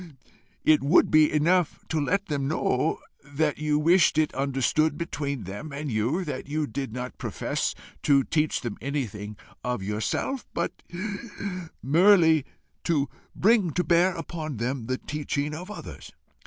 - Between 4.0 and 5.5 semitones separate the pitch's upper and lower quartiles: No, average, 3.5 semitones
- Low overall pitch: No, medium, 150 Hz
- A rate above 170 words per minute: No, average, 145 wpm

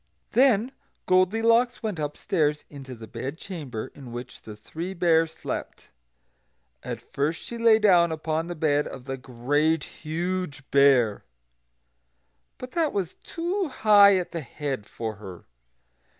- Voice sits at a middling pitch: Yes, medium, 160 Hz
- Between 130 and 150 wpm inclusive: Yes, slow, 135 wpm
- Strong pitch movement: Yes, wide, 6.6 semitones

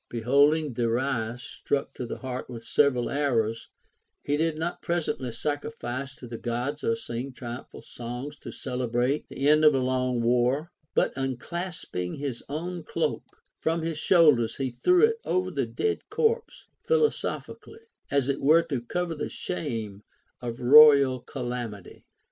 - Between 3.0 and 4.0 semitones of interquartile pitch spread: No, average, 4.4 semitones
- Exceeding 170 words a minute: No, average, 150 wpm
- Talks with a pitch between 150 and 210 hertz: No, low, 135 Hz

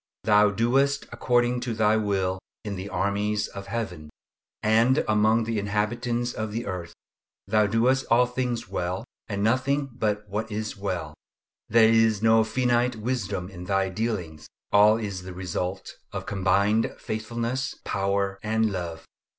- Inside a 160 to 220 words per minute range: No, average, 145 wpm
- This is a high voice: No, low, 110 Hz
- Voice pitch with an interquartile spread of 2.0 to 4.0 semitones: Yes, average, 3.0 semitones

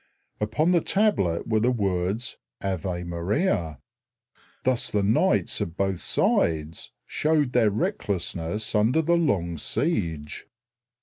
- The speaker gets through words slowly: Yes, slow, 115 wpm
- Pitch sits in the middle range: No, low, 100 Hz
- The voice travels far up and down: Yes, wide, 6.8 semitones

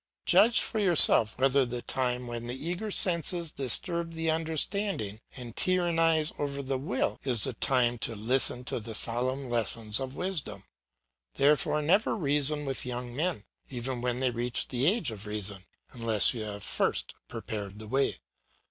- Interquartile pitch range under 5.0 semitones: No, wide, 5.4 semitones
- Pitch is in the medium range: No, low, 130 Hz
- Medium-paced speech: Yes, average, 165 wpm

